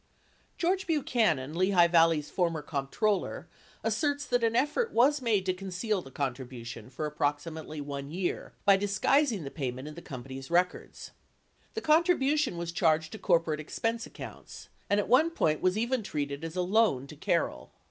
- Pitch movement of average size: No, wide, 7.6 semitones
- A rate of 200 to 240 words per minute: No, average, 165 wpm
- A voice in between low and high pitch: Yes, medium, 180 Hz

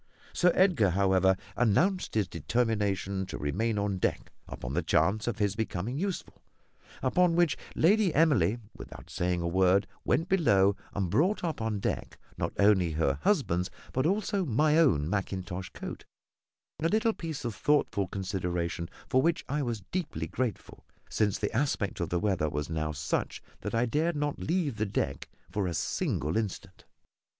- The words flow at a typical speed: Yes, average, 160 wpm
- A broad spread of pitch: Yes, wide, 8.5 semitones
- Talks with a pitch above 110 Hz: No, low, 105 Hz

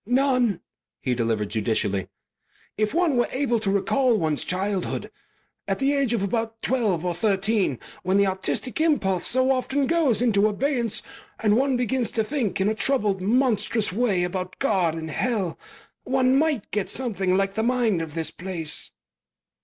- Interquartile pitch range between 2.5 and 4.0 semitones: No, wide, 5.4 semitones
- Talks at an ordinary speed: Yes, average, 160 wpm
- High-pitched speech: Yes, high, 215 Hz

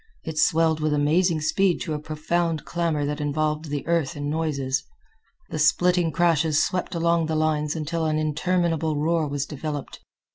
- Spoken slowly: No, average, 160 wpm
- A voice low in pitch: No, medium, 155 Hz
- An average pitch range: No, narrow, 1.9 semitones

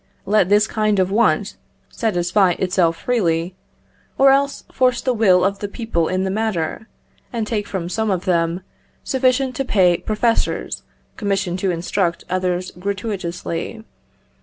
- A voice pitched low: No, high, 195 Hz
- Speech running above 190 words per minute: No, average, 145 wpm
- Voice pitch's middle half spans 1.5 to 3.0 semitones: No, average, 3.7 semitones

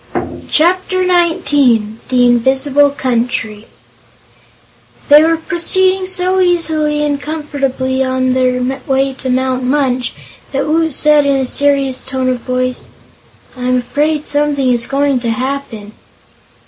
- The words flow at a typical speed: No, slow, 120 wpm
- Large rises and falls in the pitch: No, average, 3.0 semitones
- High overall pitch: Yes, very high, 275 Hz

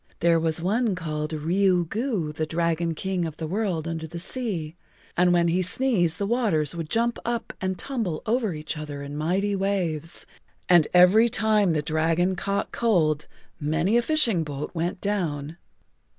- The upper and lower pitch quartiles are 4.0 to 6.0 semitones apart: Yes, average, 4.3 semitones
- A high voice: No, medium, 175 Hz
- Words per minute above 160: Yes, average, 170 wpm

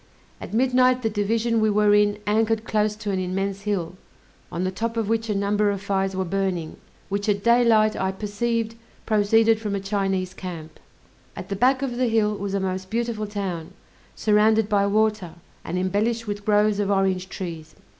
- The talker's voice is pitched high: Yes, high, 205 Hz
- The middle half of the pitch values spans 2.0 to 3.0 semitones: Yes, narrow, 2.4 semitones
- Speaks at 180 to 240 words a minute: Yes, average, 185 wpm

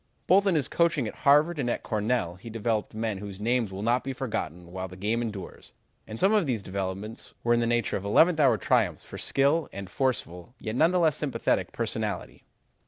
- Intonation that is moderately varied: No, wide, 5.7 semitones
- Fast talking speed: Yes, fast, 210 wpm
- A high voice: No, low, 115 Hz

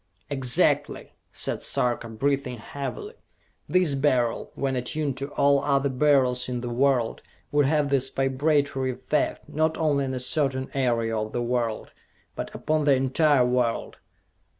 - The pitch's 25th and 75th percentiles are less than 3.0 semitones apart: Yes, narrow, 2.4 semitones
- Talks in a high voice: No, low, 135 Hz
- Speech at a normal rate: Yes, average, 145 wpm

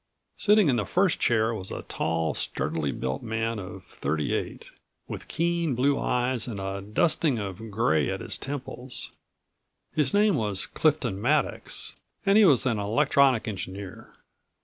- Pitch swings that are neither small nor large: No, wide, 6.4 semitones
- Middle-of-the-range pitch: No, low, 115 Hz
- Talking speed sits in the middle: Yes, average, 150 wpm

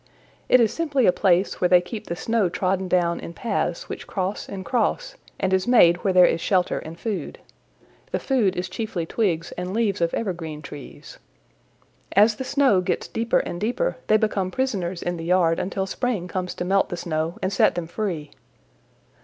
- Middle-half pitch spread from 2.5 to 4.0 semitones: Yes, average, 3.7 semitones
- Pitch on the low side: No, medium, 185 Hz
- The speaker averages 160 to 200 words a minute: Yes, average, 190 wpm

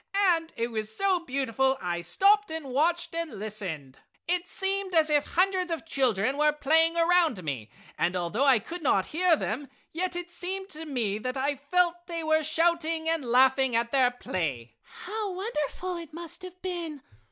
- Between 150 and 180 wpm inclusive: Yes, average, 175 wpm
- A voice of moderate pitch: No, very high, 315 Hz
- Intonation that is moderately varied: No, wide, 5.9 semitones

